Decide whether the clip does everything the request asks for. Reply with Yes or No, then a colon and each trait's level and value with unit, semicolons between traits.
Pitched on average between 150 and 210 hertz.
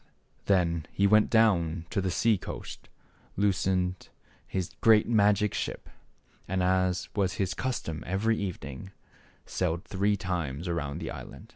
No: very low, 95 Hz